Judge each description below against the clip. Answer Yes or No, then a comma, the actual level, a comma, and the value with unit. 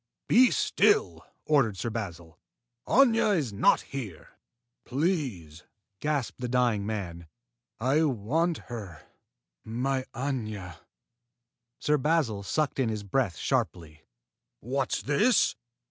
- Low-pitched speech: Yes, low, 125 Hz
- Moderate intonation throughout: No, wide, 6.8 semitones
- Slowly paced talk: Yes, slow, 105 wpm